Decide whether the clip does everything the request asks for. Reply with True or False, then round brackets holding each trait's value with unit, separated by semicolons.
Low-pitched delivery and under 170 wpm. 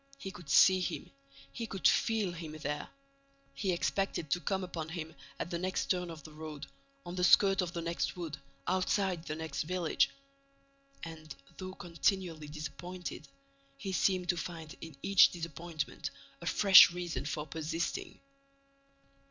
False (175 Hz; 150 wpm)